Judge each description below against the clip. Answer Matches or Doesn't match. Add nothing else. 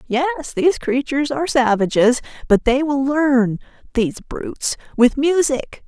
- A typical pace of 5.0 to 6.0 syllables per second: Doesn't match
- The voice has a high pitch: Matches